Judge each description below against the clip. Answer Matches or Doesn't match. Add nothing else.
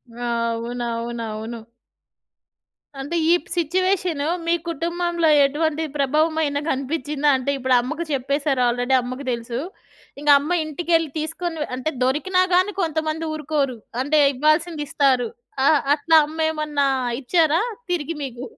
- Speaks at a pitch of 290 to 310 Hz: Matches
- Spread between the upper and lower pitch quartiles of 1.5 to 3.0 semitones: Doesn't match